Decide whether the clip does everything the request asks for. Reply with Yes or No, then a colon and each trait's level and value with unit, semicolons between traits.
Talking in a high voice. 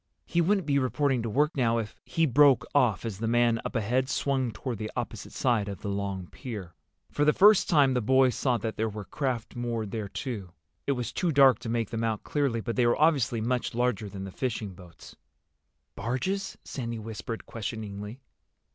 No: low, 120 Hz